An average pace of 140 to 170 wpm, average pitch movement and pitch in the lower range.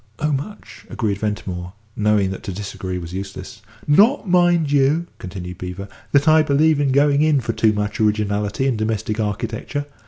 No: average, 165 wpm; wide, 6.4 semitones; low, 110 Hz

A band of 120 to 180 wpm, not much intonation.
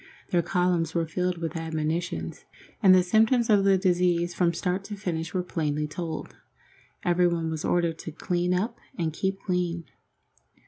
Yes: average, 155 wpm; narrow, 2.1 semitones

